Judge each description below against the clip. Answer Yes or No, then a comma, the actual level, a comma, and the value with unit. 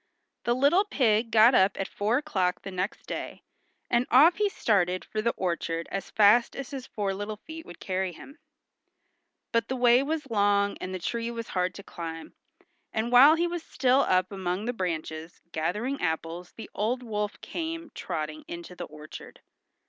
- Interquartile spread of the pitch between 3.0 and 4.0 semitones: No, wide, 5.6 semitones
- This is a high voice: Yes, high, 210 Hz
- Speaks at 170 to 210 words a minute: Yes, average, 180 wpm